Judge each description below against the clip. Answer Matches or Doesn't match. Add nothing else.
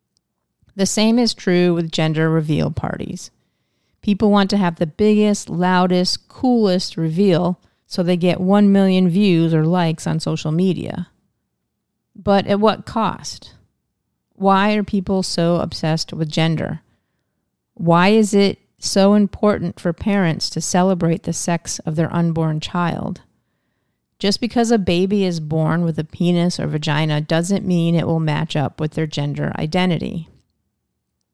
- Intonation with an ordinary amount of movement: Matches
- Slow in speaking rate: Doesn't match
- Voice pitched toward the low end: Doesn't match